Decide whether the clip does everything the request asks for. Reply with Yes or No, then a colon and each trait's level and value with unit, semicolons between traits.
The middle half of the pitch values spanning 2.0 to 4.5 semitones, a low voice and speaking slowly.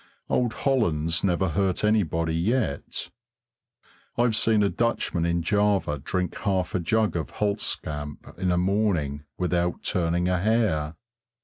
Yes: average, 4.2 semitones; very low, 90 Hz; slow, 130 wpm